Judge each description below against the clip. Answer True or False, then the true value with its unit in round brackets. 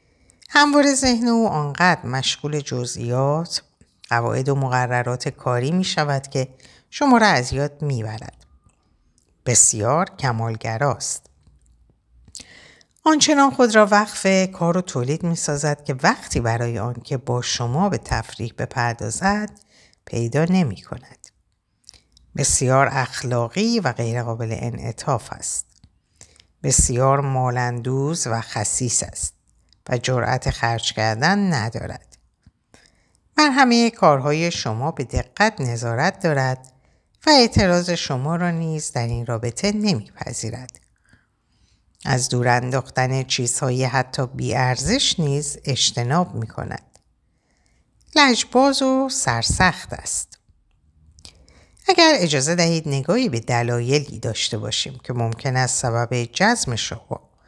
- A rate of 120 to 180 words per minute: False (110 wpm)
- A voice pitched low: True (130 Hz)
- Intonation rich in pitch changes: True (6.2 semitones)